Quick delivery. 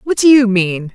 Yes: fast, 255 wpm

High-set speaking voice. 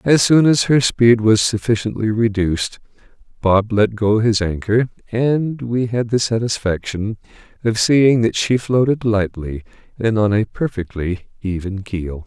No: low, 110 Hz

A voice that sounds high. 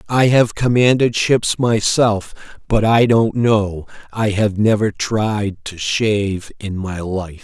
No: low, 105 Hz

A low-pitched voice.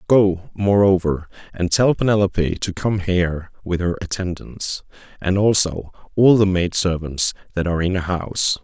Yes: very low, 95 Hz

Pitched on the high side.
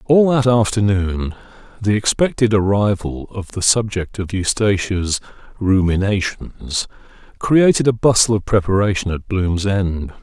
No: low, 100 Hz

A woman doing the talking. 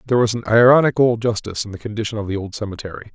No: male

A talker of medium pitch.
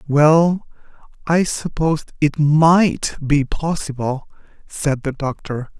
Yes: medium, 150 Hz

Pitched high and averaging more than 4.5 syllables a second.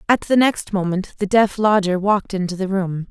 Yes: high, 195 Hz; 5.2 syllables/s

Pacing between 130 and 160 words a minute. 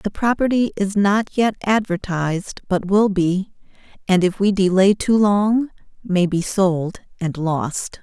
Yes: average, 150 wpm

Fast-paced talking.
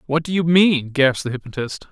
Yes: fast, 220 wpm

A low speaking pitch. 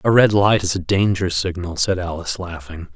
Yes: very low, 90 Hz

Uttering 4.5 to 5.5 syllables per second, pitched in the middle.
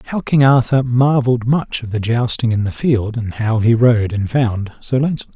No: 5.0 syllables/s; low, 120 Hz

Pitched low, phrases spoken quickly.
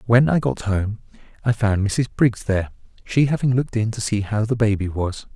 Yes: low, 110 Hz; fast, 215 wpm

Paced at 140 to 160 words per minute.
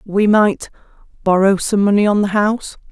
Yes: average, 145 wpm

